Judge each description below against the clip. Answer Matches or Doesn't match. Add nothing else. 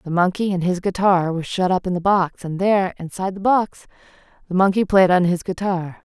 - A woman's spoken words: Matches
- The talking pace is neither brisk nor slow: Doesn't match